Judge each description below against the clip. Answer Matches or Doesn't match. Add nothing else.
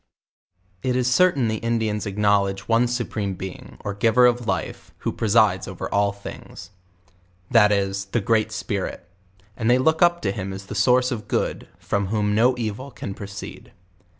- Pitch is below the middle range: Matches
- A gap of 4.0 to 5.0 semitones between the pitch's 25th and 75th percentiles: Doesn't match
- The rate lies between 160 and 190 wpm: Matches